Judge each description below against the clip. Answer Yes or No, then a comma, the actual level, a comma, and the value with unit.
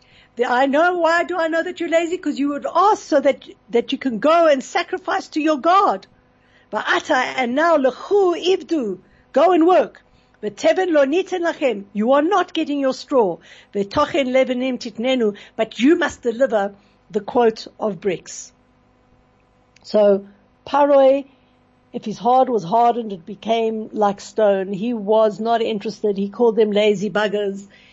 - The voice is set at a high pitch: Yes, very high, 260 Hz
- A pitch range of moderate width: No, wide, 6.7 semitones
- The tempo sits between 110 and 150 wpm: Yes, average, 145 wpm